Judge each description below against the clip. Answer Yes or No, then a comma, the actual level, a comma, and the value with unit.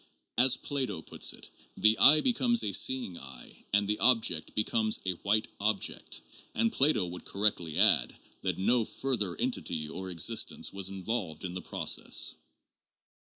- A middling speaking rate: Yes, average, 155 wpm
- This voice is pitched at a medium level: No, low, 105 Hz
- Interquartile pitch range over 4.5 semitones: Yes, wide, 5.4 semitones